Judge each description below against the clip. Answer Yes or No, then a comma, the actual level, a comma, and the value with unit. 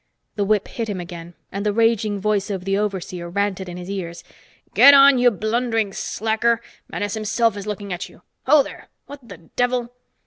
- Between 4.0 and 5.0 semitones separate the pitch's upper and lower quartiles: No, average, 3.2 semitones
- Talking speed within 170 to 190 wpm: Yes, average, 185 wpm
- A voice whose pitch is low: No, high, 205 Hz